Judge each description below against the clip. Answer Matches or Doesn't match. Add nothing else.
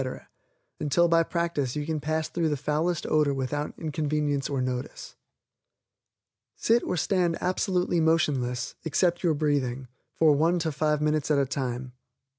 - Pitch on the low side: Doesn't match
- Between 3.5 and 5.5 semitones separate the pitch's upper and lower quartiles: Doesn't match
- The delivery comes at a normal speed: Matches